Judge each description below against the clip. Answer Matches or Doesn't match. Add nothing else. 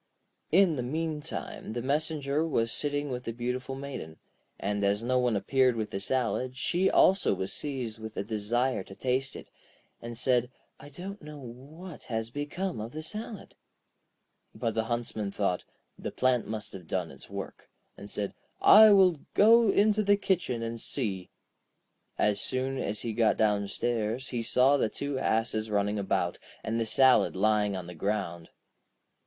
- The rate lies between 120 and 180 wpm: Matches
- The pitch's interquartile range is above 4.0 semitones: Matches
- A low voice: Matches